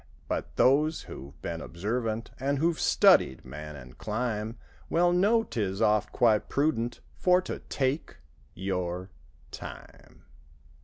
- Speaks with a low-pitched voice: Yes, low, 110 Hz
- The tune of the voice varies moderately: No, wide, 7.7 semitones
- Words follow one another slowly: Yes, slow, 110 wpm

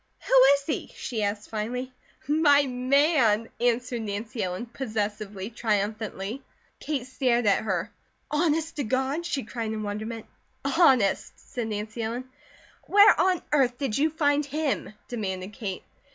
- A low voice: No, high, 240 Hz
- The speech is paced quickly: No, average, 140 wpm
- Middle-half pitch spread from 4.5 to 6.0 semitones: Yes, average, 4.9 semitones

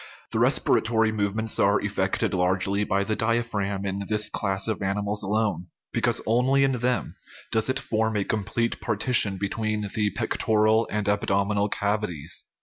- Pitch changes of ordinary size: No, narrow, 1.9 semitones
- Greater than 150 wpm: No, average, 145 wpm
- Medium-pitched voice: No, low, 105 Hz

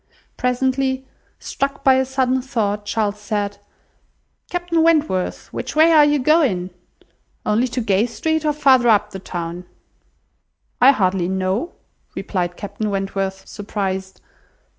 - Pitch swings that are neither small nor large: No, wide, 5.7 semitones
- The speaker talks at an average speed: No, slow, 125 wpm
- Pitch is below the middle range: No, high, 220 Hz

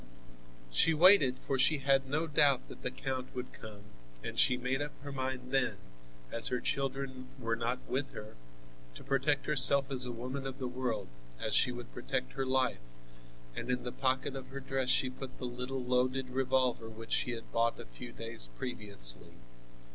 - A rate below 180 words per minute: No, average, 185 wpm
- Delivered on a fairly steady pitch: Yes, narrow, 1.5 semitones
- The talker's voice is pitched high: No, low, 130 Hz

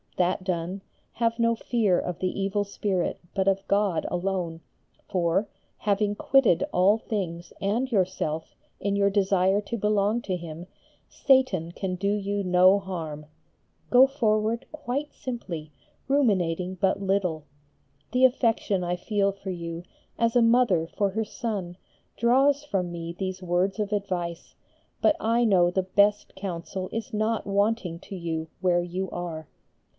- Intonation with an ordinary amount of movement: Yes, average, 3.5 semitones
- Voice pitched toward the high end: Yes, high, 195 Hz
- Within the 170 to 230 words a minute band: No, average, 145 wpm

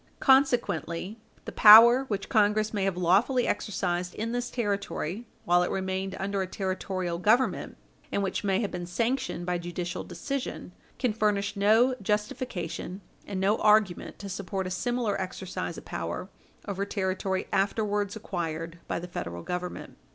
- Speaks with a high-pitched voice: Yes, high, 200 Hz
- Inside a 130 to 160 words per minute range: Yes, average, 150 wpm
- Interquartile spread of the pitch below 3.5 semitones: Yes, average, 3.1 semitones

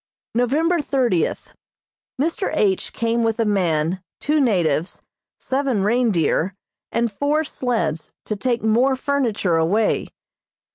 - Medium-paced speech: No, slow, 110 wpm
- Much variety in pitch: Yes, wide, 5.9 semitones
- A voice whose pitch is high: Yes, high, 230 Hz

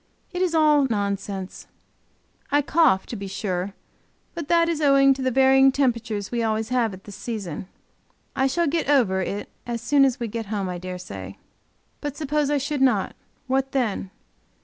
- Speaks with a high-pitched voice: Yes, very high, 255 Hz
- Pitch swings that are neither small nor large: No, wide, 5.8 semitones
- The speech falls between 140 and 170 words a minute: No, average, 185 wpm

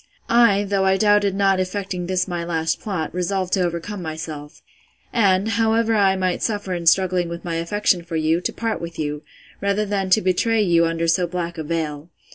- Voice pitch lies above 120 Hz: Yes, medium, 185 Hz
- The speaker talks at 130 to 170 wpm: No, average, 195 wpm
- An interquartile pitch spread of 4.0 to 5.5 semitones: No, average, 3.1 semitones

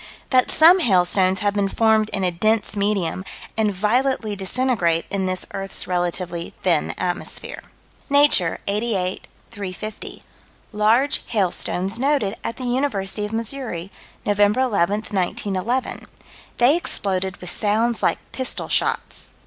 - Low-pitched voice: No, high, 205 Hz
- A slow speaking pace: Yes, slow, 125 wpm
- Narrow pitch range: No, average, 4.0 semitones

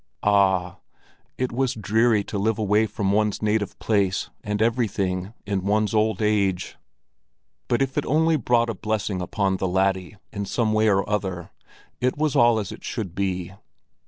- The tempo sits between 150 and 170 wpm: Yes, average, 165 wpm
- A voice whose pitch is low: Yes, low, 105 Hz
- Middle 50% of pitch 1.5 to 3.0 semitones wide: Yes, narrow, 2.6 semitones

